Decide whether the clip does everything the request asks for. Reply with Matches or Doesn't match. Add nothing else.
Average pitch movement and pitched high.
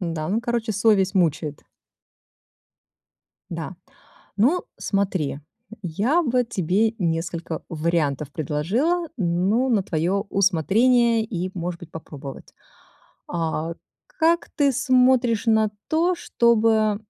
Doesn't match